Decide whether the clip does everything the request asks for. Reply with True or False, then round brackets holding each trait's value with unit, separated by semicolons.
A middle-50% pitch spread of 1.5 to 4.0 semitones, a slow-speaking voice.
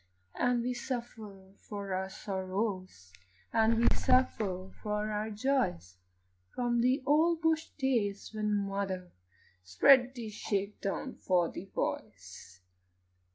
False (4.5 semitones; 115 wpm)